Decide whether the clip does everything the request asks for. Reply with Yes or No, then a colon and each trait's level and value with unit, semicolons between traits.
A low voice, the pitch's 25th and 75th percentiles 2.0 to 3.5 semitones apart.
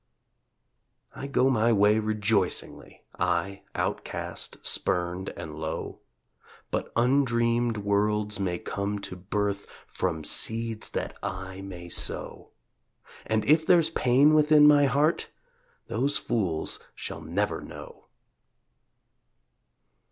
No: low, 105 Hz; average, 4.9 semitones